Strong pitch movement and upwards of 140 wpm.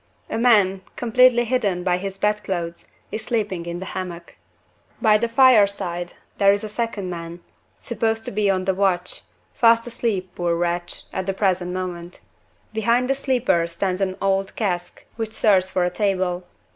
No: average, 3.7 semitones; average, 165 wpm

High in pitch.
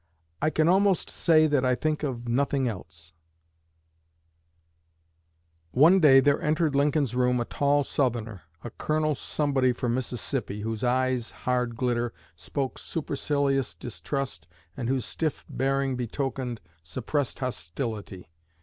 No: low, 130 Hz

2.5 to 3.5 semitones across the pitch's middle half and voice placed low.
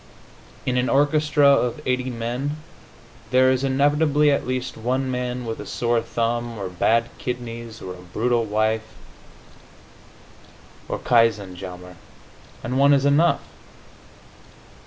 Yes: average, 3.0 semitones; low, 125 Hz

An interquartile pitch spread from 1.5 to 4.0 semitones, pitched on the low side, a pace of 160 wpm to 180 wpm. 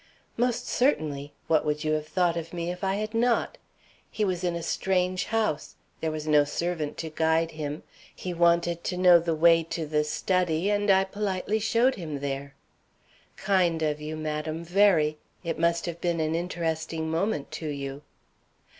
No: average, 3.1 semitones; medium, 170 Hz; average, 175 wpm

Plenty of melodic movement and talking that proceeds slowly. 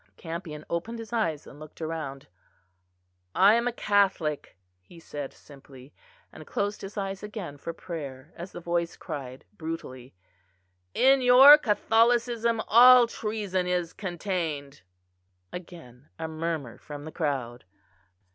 Yes: wide, 6.2 semitones; slow, 130 wpm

